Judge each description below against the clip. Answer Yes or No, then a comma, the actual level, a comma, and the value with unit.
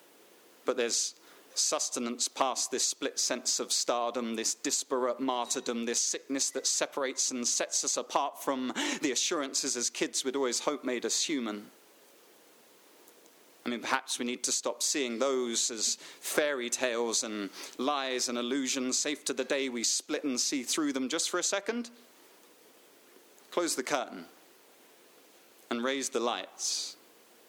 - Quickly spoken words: No, average, 150 wpm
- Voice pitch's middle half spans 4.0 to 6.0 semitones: Yes, average, 4.3 semitones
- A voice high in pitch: No, low, 130 Hz